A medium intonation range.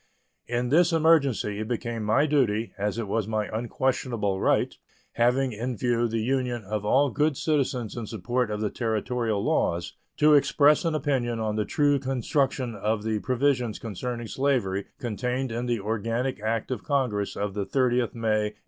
Yes: average, 3.6 semitones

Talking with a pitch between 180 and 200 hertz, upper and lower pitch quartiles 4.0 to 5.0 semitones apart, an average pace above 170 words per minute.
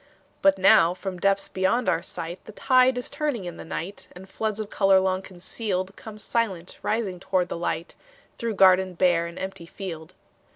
No: high, 190 Hz; average, 3.0 semitones; average, 180 wpm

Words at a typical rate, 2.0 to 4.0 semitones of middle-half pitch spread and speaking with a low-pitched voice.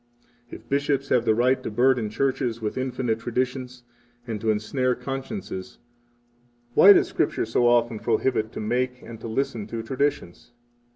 Yes: average, 160 wpm; average, 2.8 semitones; low, 120 Hz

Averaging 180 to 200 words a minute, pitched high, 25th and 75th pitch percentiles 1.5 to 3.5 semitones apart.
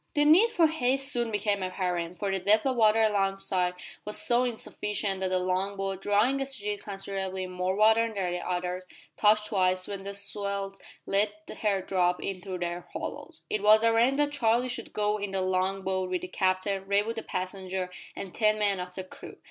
Yes: average, 195 wpm; high, 200 Hz; narrow, 2.6 semitones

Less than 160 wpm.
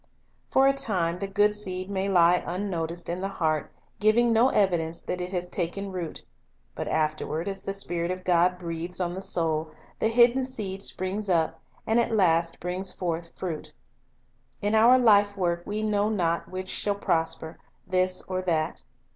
No: average, 170 wpm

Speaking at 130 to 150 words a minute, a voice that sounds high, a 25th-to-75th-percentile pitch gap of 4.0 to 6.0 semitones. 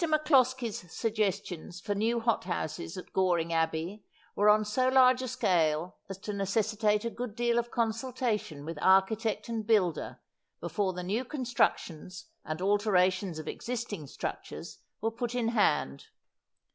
Yes: average, 145 wpm; high, 210 Hz; average, 4.5 semitones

